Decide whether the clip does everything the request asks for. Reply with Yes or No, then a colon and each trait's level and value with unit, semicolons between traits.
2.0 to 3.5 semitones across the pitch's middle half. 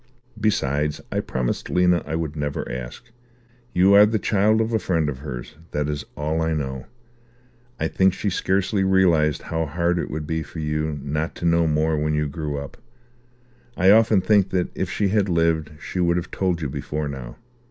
No: average, 4.0 semitones